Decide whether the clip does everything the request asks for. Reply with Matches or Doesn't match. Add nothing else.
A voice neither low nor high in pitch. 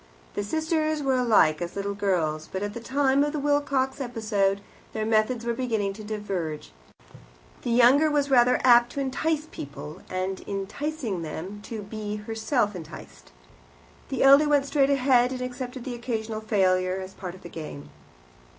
Doesn't match